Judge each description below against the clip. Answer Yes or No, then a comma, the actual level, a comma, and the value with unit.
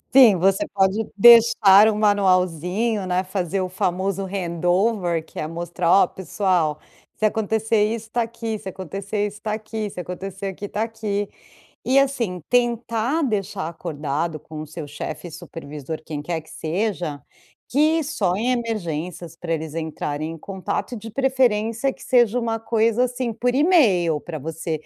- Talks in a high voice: Yes, high, 195 Hz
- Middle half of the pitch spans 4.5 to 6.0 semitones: Yes, average, 4.8 semitones